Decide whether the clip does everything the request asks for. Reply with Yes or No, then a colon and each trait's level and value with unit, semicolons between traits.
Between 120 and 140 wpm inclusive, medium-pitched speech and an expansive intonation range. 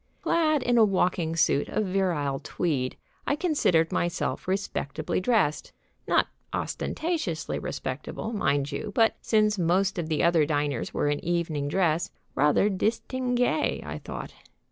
Yes: slow, 135 wpm; medium, 175 Hz; wide, 6.1 semitones